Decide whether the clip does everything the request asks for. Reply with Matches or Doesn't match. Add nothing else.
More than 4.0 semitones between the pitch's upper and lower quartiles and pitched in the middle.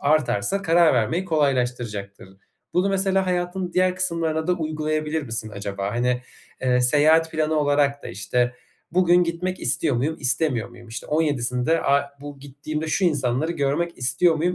Matches